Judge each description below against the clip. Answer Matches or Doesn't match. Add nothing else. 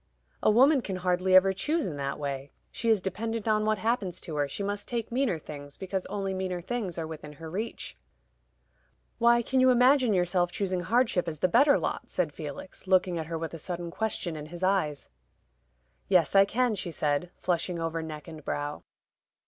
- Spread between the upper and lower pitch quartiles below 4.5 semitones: Doesn't match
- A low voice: Doesn't match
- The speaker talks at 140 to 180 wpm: Doesn't match